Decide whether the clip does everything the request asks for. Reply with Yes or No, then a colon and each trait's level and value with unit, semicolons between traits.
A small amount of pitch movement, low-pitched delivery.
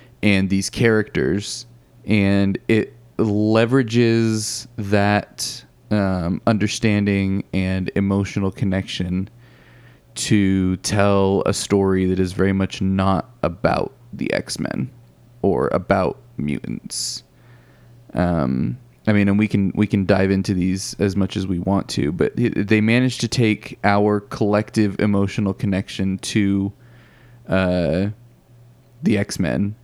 No: average, 3.1 semitones; low, 100 Hz